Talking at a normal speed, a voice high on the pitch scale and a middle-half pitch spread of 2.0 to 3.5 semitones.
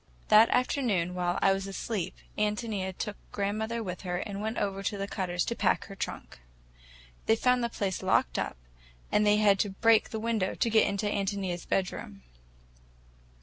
Yes: average, 175 wpm; high, 200 Hz; narrow, 2.6 semitones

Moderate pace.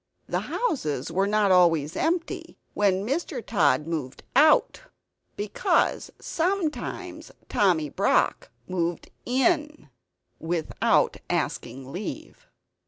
No: slow, 95 wpm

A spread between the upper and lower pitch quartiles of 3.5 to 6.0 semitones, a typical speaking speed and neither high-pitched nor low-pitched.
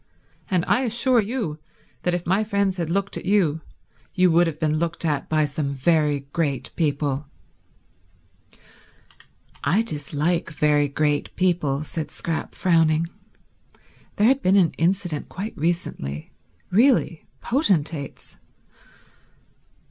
No: average, 4.2 semitones; slow, 120 wpm; medium, 165 Hz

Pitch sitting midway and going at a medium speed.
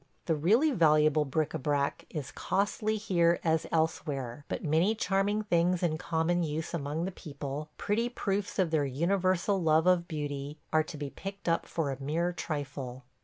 Yes: medium, 160 Hz; average, 170 wpm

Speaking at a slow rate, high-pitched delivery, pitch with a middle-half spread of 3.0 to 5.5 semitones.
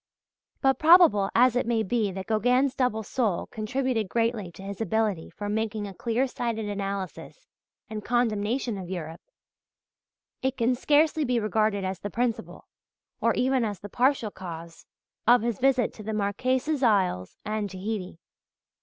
No: average, 155 wpm; high, 220 Hz; average, 3.7 semitones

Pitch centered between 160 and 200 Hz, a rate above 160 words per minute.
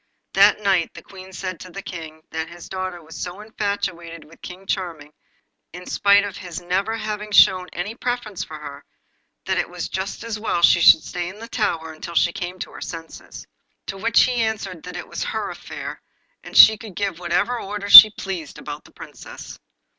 Yes: medium, 185 Hz; average, 200 wpm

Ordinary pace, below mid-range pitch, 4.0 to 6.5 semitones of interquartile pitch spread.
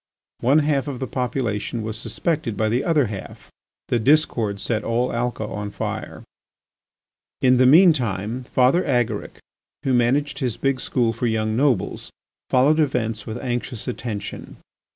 No: average, 150 wpm; low, 125 Hz; average, 3.5 semitones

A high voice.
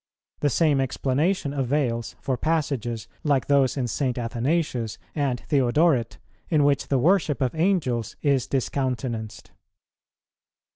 No: low, 135 Hz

